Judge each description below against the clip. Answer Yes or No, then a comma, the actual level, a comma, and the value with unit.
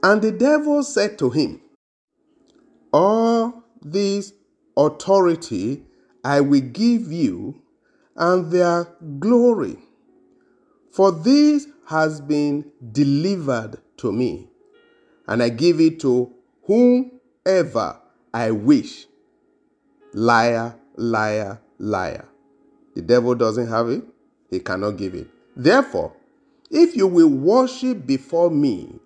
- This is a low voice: No, medium, 180 Hz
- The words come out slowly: Yes, slow, 105 wpm